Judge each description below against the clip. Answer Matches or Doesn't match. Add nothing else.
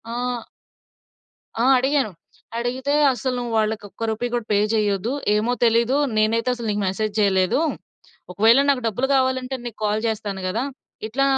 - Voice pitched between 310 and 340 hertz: Doesn't match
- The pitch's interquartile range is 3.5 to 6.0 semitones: Doesn't match